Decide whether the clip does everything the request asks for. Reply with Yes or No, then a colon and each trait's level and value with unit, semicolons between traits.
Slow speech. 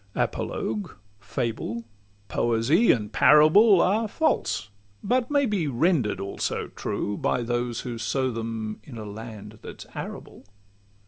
Yes: slow, 130 wpm